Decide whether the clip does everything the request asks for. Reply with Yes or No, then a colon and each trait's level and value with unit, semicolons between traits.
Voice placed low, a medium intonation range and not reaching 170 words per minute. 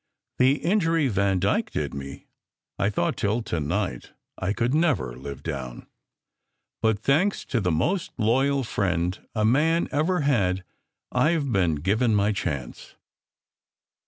No: low, 105 Hz; wide, 7.9 semitones; slow, 135 wpm